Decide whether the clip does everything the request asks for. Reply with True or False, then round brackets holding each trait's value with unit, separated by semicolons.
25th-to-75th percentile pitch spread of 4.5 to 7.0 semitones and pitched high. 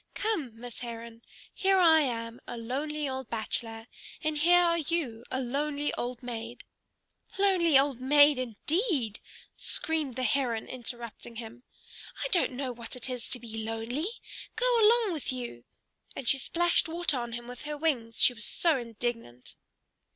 True (4.9 semitones; 255 Hz)